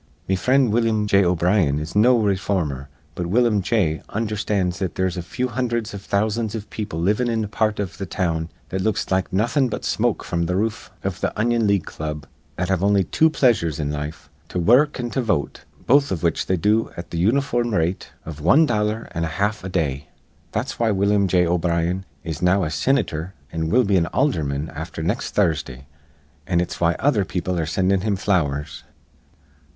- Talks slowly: No, average, 200 wpm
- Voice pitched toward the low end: Yes, very low, 95 Hz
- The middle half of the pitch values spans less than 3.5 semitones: No, average, 4.6 semitones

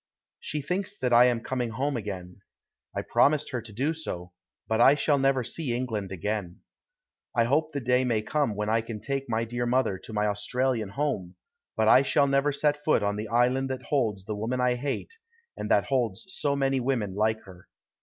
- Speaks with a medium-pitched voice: No, low, 125 Hz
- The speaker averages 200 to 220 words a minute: Yes, fast, 205 wpm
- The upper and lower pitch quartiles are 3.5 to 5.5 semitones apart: Yes, average, 4.3 semitones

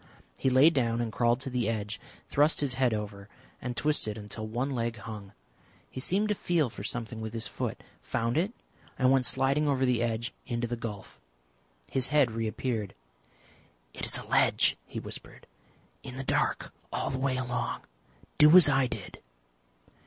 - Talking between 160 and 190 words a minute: Yes, average, 175 wpm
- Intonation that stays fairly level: No, average, 3.0 semitones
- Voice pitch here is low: Yes, low, 125 Hz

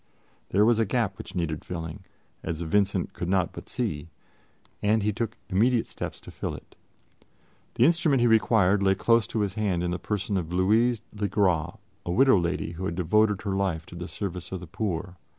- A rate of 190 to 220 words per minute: Yes, average, 200 wpm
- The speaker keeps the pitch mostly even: No, average, 3.7 semitones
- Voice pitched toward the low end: Yes, very low, 95 Hz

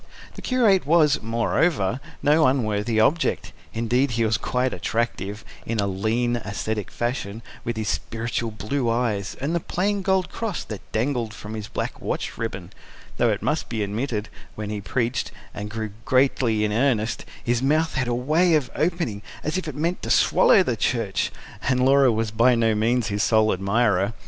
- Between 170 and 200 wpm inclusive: Yes, average, 175 wpm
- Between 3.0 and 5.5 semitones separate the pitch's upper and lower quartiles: Yes, average, 4.2 semitones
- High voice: No, low, 115 Hz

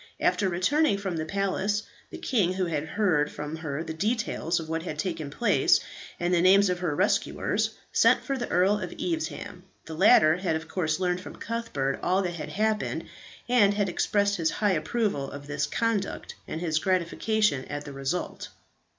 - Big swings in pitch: No, average, 4.4 semitones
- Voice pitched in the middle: Yes, medium, 180 Hz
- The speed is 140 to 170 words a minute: No, average, 185 wpm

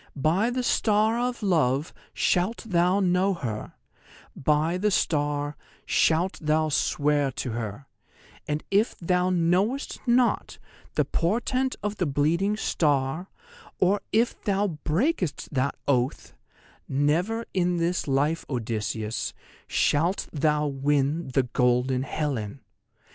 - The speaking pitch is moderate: Yes, medium, 160 Hz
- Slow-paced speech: Yes, slow, 120 wpm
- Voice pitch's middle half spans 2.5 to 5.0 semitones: No, wide, 5.6 semitones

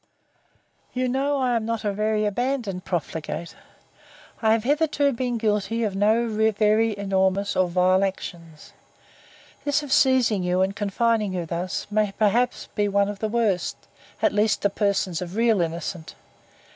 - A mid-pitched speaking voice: No, high, 210 Hz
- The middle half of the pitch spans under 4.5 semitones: Yes, average, 3.4 semitones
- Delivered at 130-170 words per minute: Yes, average, 155 wpm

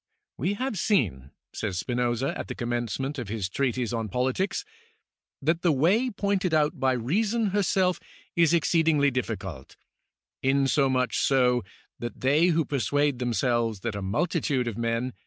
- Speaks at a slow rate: No, average, 150 wpm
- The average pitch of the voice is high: No, low, 130 Hz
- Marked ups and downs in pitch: Yes, wide, 5.9 semitones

